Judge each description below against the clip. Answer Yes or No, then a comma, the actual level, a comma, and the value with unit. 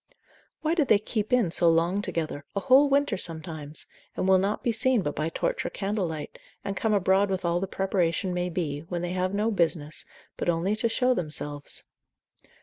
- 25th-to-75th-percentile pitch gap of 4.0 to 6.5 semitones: Yes, average, 4.4 semitones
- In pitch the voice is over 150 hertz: Yes, medium, 185 Hz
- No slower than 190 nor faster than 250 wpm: Yes, average, 195 wpm